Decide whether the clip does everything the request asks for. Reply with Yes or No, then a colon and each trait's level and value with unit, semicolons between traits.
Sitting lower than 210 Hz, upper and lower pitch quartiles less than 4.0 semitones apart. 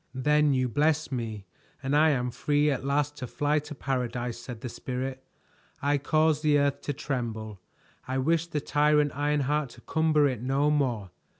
Yes: medium, 140 Hz; average, 2.9 semitones